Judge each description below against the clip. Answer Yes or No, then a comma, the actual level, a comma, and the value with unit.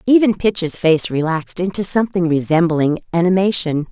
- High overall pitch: No, medium, 175 Hz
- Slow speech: Yes, slow, 125 wpm